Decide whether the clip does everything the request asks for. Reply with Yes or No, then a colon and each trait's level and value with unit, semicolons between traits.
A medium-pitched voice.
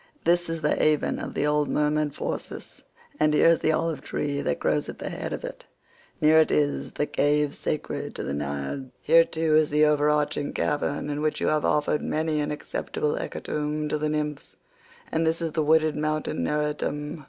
Yes: medium, 150 Hz